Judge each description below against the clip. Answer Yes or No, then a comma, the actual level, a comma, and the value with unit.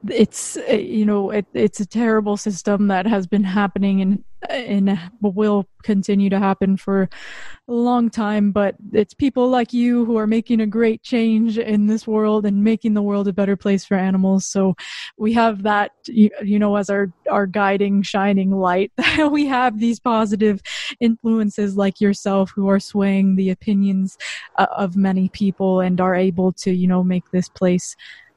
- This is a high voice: Yes, high, 205 Hz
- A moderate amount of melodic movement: No, narrow, 2.1 semitones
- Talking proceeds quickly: No, average, 175 wpm